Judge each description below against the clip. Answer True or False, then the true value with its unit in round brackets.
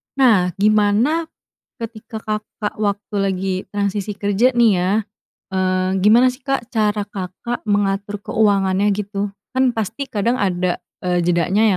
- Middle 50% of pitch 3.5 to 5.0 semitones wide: False (2.8 semitones)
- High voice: True (205 Hz)